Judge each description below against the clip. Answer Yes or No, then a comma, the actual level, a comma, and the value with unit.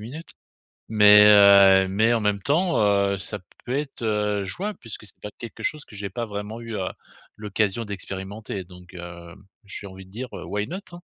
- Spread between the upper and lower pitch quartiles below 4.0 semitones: Yes, average, 2.9 semitones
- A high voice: No, low, 105 Hz